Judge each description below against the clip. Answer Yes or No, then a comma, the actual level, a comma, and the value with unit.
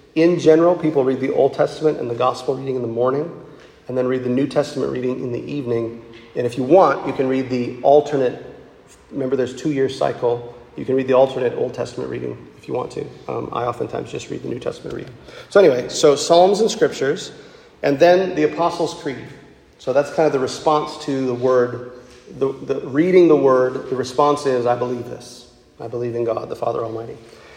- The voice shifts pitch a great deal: No, average, 3.4 semitones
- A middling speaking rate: No, fast, 210 wpm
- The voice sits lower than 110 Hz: No, low, 130 Hz